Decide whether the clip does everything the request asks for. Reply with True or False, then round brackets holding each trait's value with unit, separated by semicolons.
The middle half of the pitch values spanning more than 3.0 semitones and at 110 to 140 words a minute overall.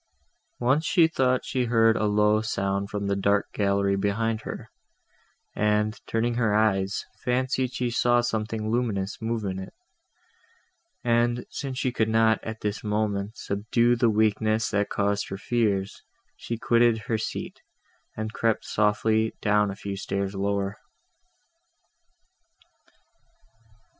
False (2.5 semitones; 135 wpm)